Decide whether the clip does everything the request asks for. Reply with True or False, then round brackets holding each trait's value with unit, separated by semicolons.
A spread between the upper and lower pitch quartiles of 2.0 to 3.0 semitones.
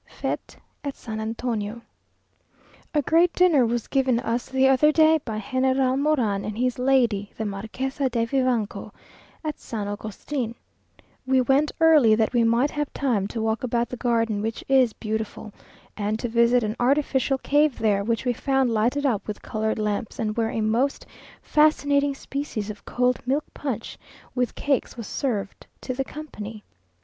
False (3.7 semitones)